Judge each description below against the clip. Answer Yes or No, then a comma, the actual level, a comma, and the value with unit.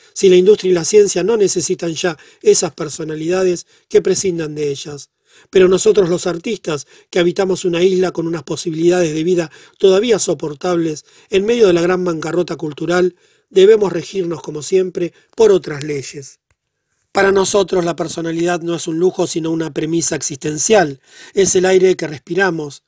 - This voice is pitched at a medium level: Yes, medium, 175 Hz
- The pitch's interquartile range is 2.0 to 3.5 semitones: Yes, average, 2.8 semitones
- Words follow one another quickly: No, average, 160 wpm